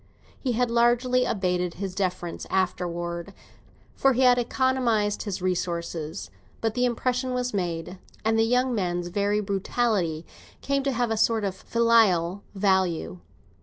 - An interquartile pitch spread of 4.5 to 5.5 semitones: Yes, average, 5.2 semitones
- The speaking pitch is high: Yes, high, 205 Hz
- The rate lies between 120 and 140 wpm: Yes, slow, 135 wpm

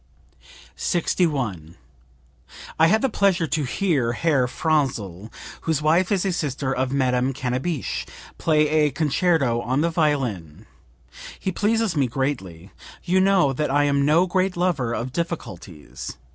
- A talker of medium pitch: Yes, medium, 145 Hz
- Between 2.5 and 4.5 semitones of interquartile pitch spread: No, average, 5.3 semitones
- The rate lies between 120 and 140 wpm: Yes, slow, 135 wpm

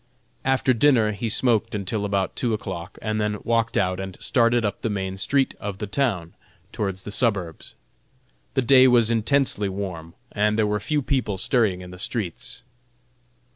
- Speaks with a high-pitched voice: No, low, 105 Hz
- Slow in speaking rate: No, average, 170 wpm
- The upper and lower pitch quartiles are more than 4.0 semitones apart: No, average, 3.7 semitones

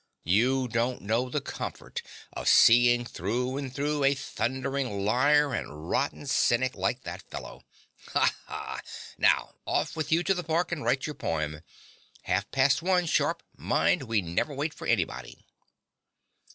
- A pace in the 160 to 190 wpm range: No, average, 150 wpm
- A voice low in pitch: Yes, low, 130 Hz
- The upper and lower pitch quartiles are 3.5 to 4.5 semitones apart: No, average, 5.3 semitones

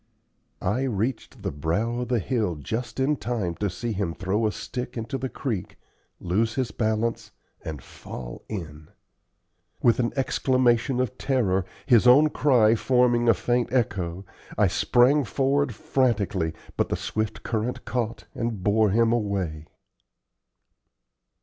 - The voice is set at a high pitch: No, low, 115 Hz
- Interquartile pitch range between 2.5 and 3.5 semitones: No, average, 3.9 semitones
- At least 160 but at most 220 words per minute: No, average, 140 wpm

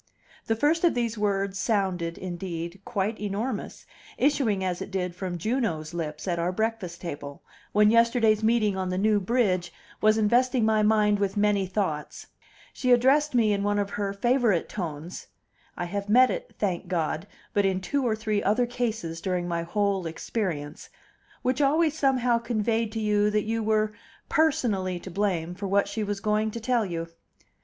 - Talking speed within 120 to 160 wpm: No, average, 175 wpm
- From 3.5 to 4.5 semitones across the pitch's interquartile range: Yes, average, 3.8 semitones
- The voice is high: Yes, high, 205 Hz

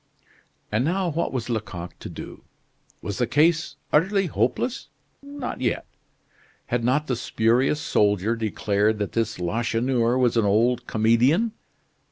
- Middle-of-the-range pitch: No, low, 120 Hz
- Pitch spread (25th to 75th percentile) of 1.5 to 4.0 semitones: No, wide, 5.4 semitones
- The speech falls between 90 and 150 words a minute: Yes, slow, 135 wpm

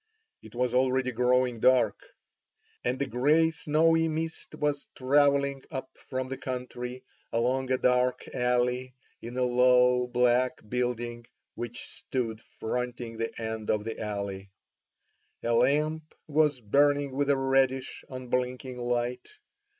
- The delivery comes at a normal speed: No, slow, 125 wpm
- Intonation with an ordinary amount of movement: No, narrow, 1.8 semitones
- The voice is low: Yes, low, 125 Hz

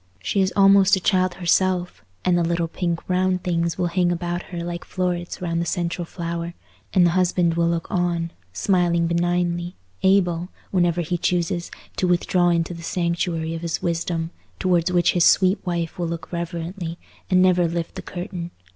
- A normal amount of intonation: No, narrow, 1.2 semitones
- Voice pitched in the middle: Yes, medium, 175 Hz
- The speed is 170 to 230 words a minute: Yes, average, 175 wpm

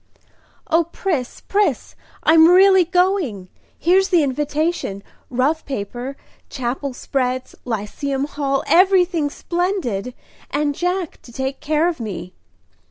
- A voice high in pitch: Yes, very high, 295 Hz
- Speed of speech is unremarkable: No, slow, 110 wpm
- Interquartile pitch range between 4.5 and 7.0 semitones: Yes, wide, 5.6 semitones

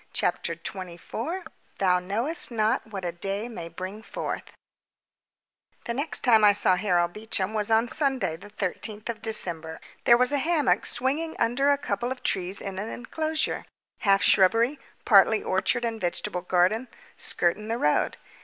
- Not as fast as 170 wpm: Yes, average, 160 wpm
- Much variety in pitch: No, average, 4.5 semitones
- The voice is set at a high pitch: Yes, high, 215 Hz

